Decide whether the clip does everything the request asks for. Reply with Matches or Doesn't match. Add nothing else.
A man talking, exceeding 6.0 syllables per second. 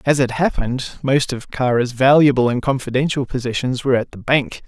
Doesn't match